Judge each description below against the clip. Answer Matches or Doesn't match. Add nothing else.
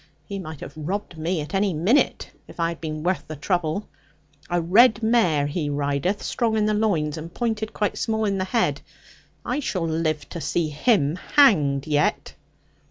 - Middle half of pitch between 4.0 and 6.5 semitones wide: Matches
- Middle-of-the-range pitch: Matches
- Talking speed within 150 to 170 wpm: Doesn't match